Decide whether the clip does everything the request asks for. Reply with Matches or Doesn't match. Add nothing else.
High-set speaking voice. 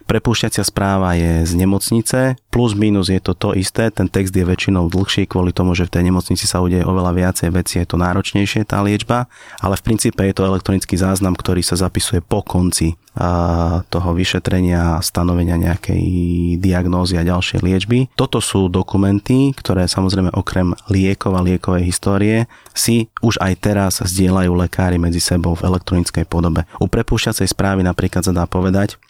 Doesn't match